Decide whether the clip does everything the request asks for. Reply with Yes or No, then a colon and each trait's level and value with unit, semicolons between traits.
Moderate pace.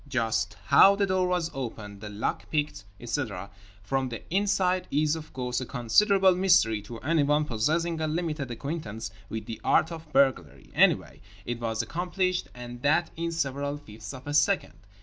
Yes: average, 170 wpm